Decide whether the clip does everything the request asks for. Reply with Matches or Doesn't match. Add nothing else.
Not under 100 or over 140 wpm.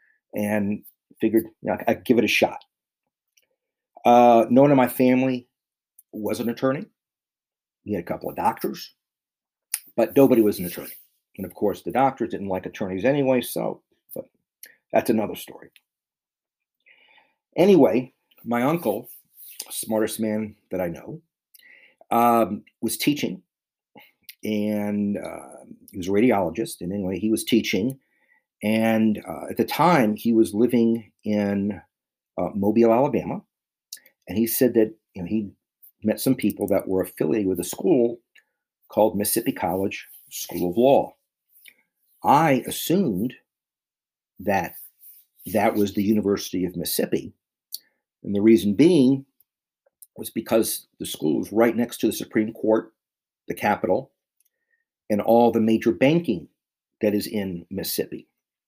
Matches